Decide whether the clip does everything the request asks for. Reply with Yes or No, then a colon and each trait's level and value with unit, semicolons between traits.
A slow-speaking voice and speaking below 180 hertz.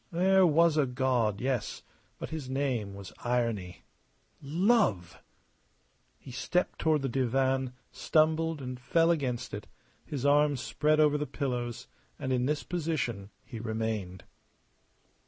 Yes: slow, 130 wpm; low, 135 Hz